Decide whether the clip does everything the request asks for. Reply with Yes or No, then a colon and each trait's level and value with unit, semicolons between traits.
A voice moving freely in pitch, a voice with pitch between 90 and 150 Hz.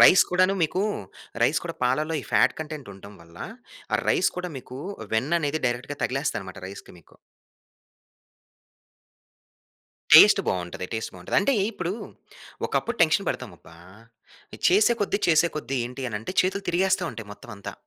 Yes: wide, 8.7 semitones; medium, 140 Hz